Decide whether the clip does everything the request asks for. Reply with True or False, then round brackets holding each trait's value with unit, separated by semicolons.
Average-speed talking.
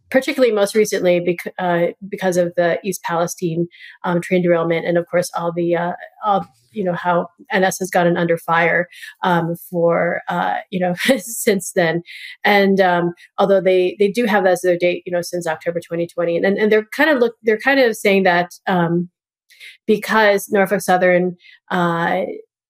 True (180 wpm)